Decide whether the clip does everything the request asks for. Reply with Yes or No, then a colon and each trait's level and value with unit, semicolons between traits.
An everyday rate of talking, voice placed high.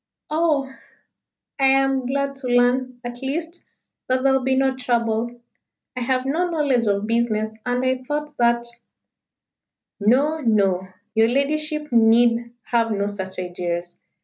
Yes: average, 145 wpm; high, 245 Hz